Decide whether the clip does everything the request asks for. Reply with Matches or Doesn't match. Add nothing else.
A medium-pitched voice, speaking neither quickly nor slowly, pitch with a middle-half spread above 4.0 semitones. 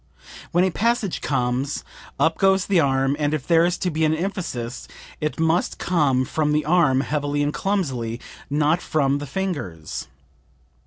Matches